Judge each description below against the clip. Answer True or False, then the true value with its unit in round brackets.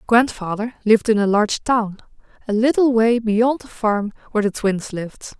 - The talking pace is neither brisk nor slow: True (180 wpm)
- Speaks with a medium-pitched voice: False (220 Hz)